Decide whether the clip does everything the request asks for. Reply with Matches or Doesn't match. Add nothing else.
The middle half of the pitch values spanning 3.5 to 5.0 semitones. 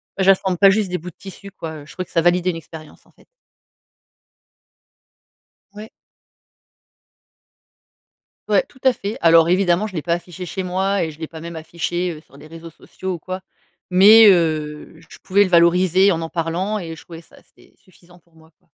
Doesn't match